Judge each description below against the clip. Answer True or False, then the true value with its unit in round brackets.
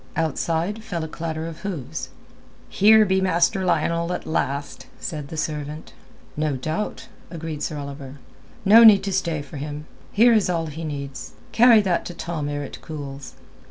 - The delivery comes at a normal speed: True (165 wpm)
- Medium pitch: True (160 Hz)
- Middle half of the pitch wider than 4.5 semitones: False (4.2 semitones)